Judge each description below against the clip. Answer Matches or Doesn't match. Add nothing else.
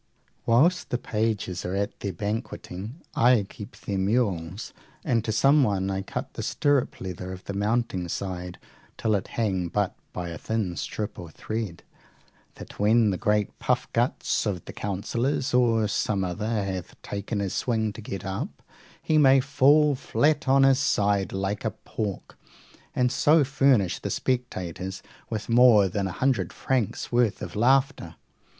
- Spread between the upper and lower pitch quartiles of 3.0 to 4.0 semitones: Doesn't match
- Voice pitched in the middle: Doesn't match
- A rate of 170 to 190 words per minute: Doesn't match